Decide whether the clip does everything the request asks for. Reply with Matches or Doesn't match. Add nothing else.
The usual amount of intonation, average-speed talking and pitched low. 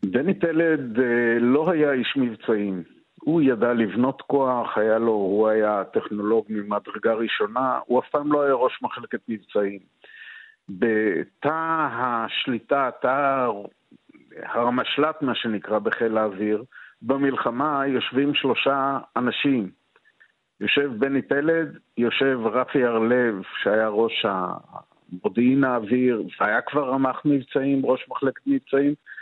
Matches